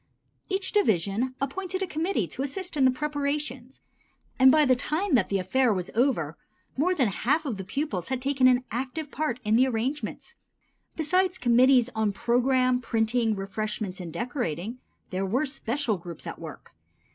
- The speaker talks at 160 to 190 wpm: Yes, average, 165 wpm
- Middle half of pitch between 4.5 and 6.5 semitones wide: Yes, average, 4.9 semitones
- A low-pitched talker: No, very high, 255 Hz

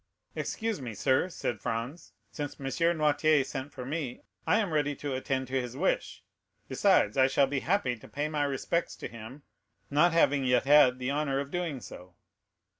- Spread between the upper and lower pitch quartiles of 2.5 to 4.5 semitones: Yes, average, 3.0 semitones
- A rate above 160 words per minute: Yes, average, 185 wpm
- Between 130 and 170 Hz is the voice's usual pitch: Yes, medium, 140 Hz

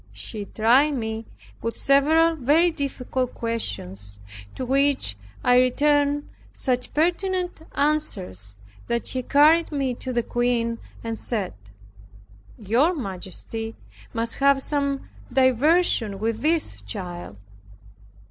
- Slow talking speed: Yes, slow, 110 wpm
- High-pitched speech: Yes, very high, 255 Hz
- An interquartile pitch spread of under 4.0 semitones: No, average, 4.6 semitones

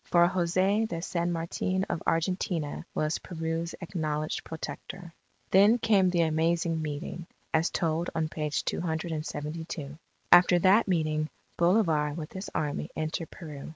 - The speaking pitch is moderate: Yes, medium, 165 Hz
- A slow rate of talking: Yes, slow, 130 wpm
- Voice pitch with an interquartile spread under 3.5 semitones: Yes, narrow, 2.4 semitones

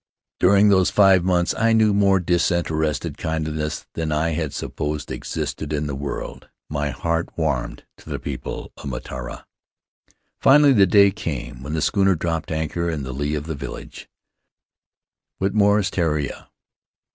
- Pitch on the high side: No, very low, 80 Hz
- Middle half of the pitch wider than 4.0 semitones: Yes, average, 4.4 semitones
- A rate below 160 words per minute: Yes, average, 150 wpm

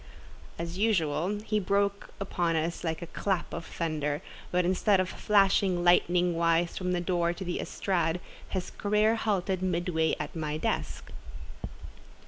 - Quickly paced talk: No, average, 145 wpm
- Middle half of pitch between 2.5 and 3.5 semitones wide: Yes, average, 2.8 semitones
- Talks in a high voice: No, medium, 180 Hz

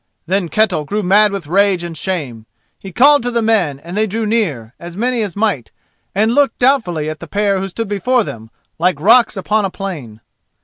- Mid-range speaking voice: No, high, 195 Hz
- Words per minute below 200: No, fast, 205 wpm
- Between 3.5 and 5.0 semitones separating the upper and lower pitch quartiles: Yes, average, 4.5 semitones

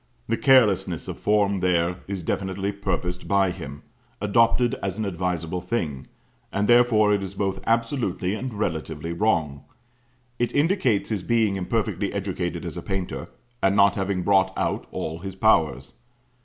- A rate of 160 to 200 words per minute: No, average, 150 wpm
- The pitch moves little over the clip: No, average, 3.2 semitones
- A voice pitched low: Yes, very low, 95 Hz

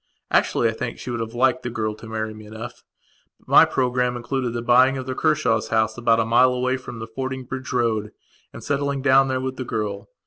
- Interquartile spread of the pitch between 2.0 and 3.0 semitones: Yes, narrow, 2.6 semitones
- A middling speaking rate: No, fast, 220 wpm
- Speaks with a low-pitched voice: Yes, low, 120 Hz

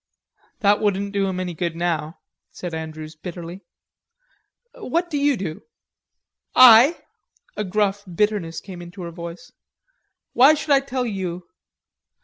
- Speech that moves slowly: Yes, slow, 130 wpm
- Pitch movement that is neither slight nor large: Yes, average, 4.5 semitones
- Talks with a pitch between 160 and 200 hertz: Yes, high, 190 Hz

